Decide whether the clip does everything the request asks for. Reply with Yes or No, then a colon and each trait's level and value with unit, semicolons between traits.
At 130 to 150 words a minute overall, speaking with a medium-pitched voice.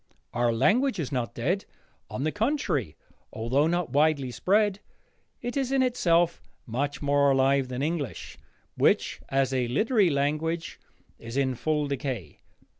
Yes: average, 140 wpm; medium, 145 Hz